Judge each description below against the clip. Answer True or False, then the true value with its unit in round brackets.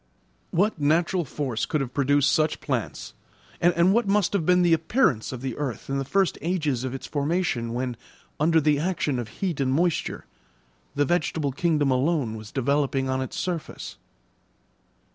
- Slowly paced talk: False (165 wpm)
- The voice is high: False (150 Hz)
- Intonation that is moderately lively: True (4.5 semitones)